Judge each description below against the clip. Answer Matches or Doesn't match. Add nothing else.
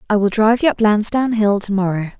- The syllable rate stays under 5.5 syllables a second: Doesn't match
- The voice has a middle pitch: Doesn't match